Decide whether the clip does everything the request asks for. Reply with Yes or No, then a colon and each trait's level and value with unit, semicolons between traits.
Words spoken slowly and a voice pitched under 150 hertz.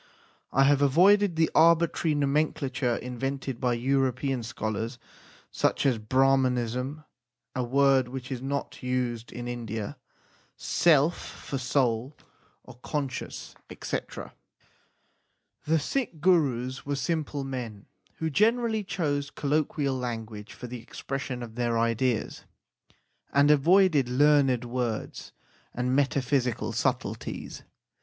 Yes: slow, 115 wpm; low, 135 Hz